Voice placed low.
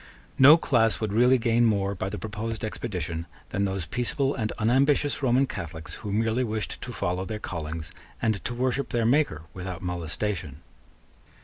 Yes: low, 110 Hz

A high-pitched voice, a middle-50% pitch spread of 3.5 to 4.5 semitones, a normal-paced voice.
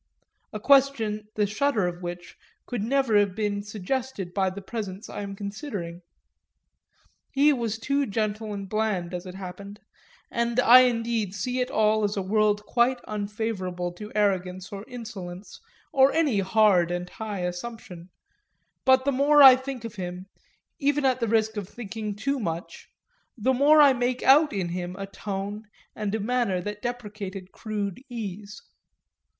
Yes: high, 210 Hz; average, 3.9 semitones; average, 160 wpm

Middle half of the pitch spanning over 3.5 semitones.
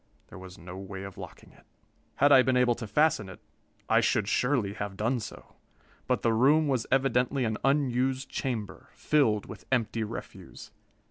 Yes: average, 4.3 semitones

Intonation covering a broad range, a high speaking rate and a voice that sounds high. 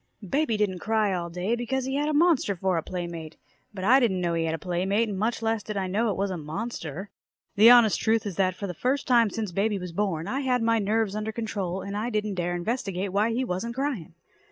No: average, 4.1 semitones; fast, 250 wpm; high, 205 Hz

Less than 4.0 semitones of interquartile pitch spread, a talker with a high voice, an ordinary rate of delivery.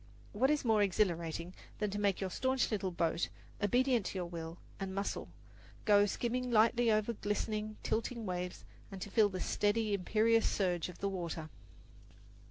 Yes: average, 3.6 semitones; high, 205 Hz; average, 165 wpm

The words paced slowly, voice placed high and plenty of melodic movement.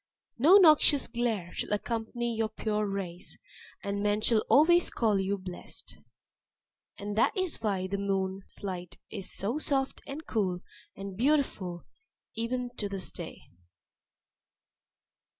No: slow, 130 wpm; high, 210 Hz; average, 4.1 semitones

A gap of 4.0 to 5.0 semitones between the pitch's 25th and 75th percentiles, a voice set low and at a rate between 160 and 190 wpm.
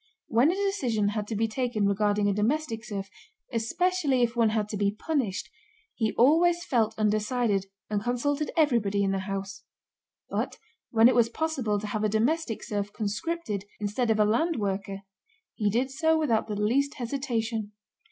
No: average, 4.4 semitones; high, 225 Hz; average, 170 wpm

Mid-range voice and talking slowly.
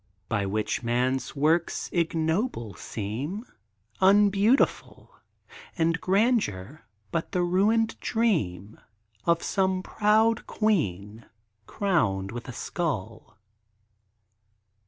Yes: medium, 165 Hz; slow, 85 wpm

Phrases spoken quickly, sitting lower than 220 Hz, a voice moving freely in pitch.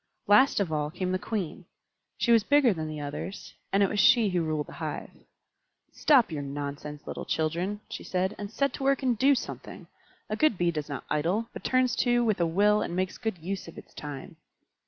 Yes: fast, 215 wpm; high, 190 Hz; wide, 6.3 semitones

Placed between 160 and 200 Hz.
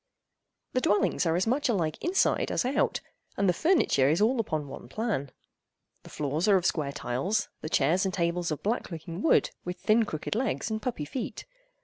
Yes: medium, 185 Hz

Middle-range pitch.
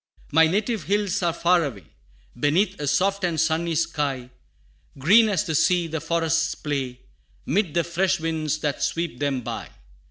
Yes: medium, 165 Hz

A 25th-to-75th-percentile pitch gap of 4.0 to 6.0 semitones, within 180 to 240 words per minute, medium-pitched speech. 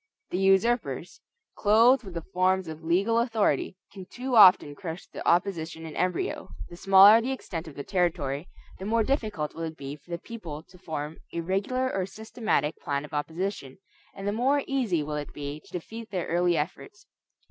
Yes: average, 5.0 semitones; average, 185 wpm; medium, 180 Hz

